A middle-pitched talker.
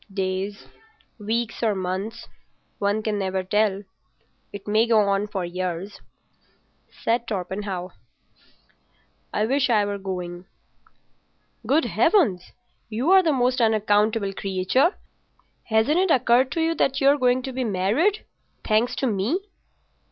No: high, 215 Hz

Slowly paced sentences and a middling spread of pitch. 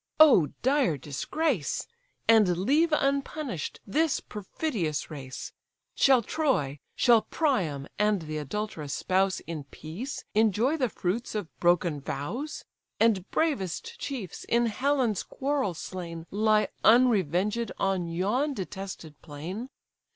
No: slow, 115 wpm; wide, 7.5 semitones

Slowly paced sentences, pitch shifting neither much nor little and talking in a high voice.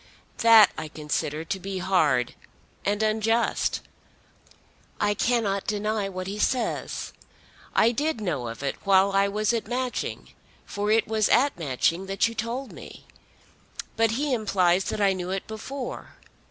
No: average, 150 wpm; average, 3.2 semitones; high, 205 Hz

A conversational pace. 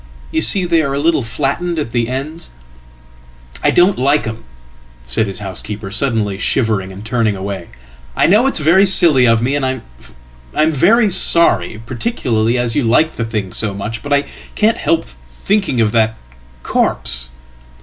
Yes: average, 155 wpm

